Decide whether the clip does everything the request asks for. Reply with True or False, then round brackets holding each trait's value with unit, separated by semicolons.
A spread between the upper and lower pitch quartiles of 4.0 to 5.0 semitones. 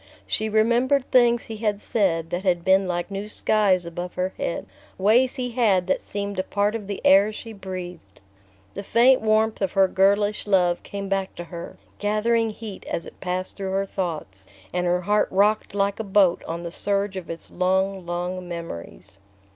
False (3.0 semitones)